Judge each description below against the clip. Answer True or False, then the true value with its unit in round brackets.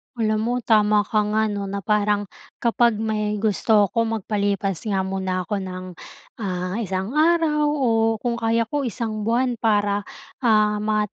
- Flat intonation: True (2.3 semitones)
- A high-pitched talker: True (215 Hz)